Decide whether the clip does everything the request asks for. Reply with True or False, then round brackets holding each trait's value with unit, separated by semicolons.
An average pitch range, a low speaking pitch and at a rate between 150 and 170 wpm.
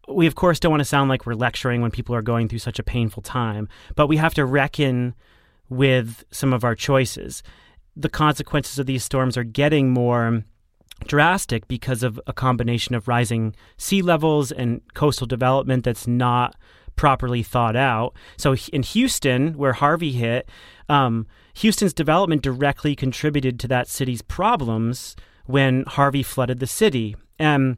True (3.3 semitones; 130 Hz; 160 wpm)